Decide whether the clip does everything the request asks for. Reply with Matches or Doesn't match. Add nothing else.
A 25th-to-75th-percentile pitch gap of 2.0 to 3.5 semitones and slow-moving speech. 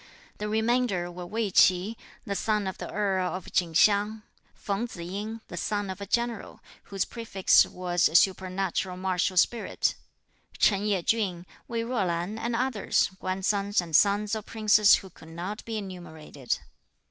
Doesn't match